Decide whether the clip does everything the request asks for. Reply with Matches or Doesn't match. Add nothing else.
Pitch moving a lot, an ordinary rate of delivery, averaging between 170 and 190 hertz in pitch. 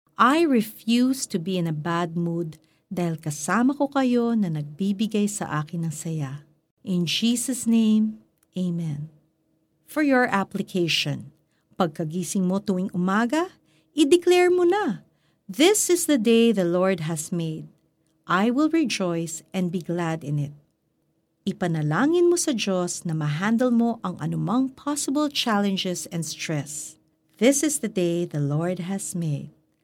Matches